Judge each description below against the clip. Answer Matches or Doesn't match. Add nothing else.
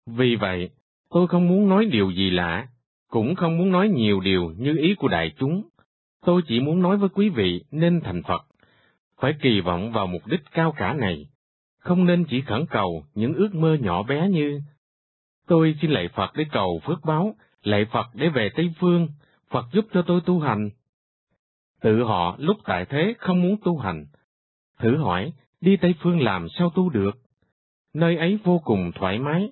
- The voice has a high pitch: Doesn't match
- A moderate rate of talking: Matches